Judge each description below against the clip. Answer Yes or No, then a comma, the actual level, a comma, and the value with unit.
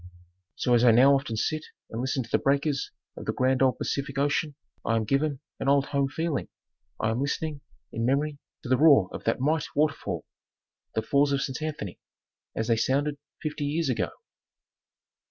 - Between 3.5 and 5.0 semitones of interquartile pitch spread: No, average, 2.8 semitones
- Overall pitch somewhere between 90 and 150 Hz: Yes, medium, 140 Hz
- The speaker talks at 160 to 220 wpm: Yes, average, 190 wpm